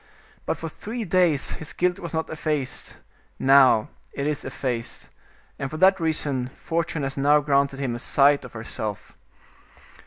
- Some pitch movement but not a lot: Yes, average, 3.3 semitones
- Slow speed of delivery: No, average, 155 wpm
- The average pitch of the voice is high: No, medium, 145 Hz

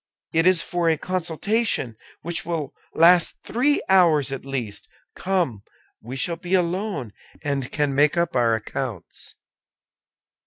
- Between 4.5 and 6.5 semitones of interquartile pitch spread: Yes, average, 5.0 semitones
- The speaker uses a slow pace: Yes, slow, 130 wpm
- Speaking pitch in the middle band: Yes, medium, 165 Hz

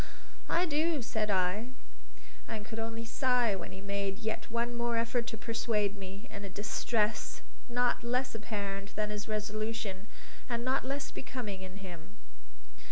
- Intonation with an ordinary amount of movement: Yes, average, 3.0 semitones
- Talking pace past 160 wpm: No, average, 155 wpm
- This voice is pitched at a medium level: No, high, 220 Hz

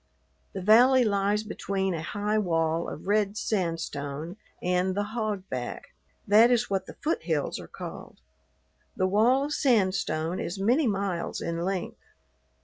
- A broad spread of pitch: No, average, 3.4 semitones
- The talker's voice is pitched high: Yes, high, 195 Hz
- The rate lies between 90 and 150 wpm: Yes, average, 140 wpm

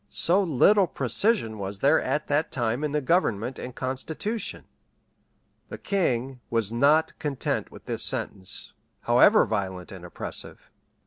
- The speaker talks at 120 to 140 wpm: Yes, slow, 135 wpm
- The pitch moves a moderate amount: No, wide, 6.3 semitones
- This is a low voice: Yes, low, 130 Hz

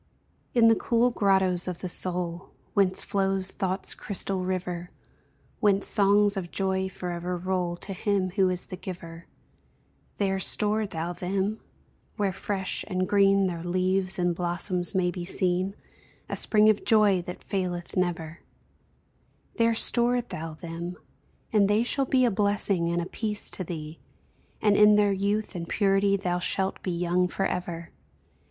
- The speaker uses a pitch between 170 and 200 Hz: Yes, high, 190 Hz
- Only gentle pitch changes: Yes, narrow, 2.3 semitones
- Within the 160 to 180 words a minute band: No, average, 150 wpm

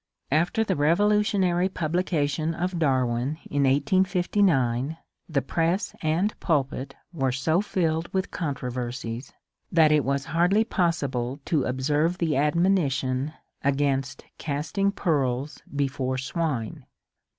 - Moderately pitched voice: Yes, medium, 150 Hz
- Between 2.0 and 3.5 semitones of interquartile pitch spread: No, average, 4.6 semitones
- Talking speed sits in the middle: No, slow, 105 wpm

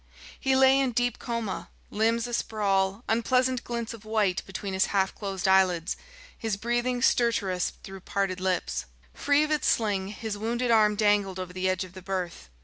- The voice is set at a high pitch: Yes, high, 210 Hz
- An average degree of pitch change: Yes, average, 3.7 semitones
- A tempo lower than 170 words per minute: No, average, 175 wpm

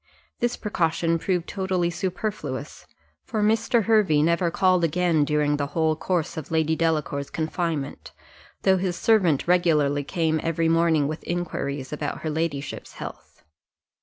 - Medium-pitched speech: Yes, medium, 165 Hz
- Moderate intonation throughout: Yes, average, 3.1 semitones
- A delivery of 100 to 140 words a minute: Yes, slow, 135 wpm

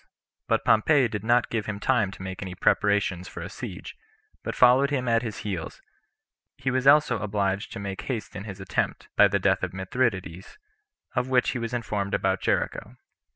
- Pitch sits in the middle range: No, low, 105 Hz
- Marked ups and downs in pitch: No, average, 4.2 semitones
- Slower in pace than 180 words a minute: No, average, 190 wpm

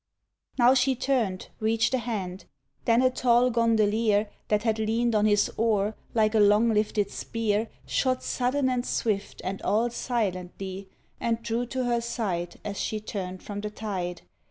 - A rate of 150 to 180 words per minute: Yes, average, 160 wpm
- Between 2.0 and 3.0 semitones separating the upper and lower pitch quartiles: Yes, narrow, 2.6 semitones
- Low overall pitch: No, high, 220 Hz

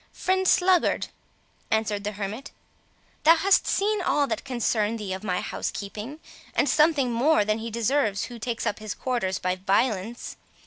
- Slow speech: No, average, 165 wpm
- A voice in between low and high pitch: No, high, 230 Hz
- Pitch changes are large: Yes, wide, 5.9 semitones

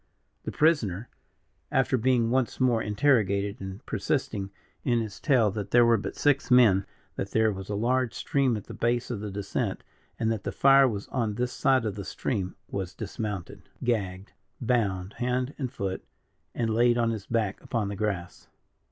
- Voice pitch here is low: Yes, low, 110 Hz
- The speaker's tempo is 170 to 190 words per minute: Yes, average, 180 wpm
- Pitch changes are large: No, average, 3.8 semitones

